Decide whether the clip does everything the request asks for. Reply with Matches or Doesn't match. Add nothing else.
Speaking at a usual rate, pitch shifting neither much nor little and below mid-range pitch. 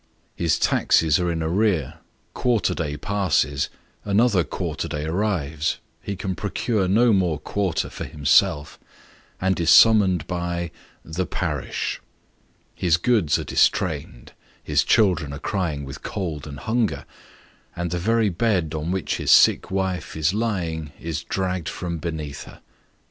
Matches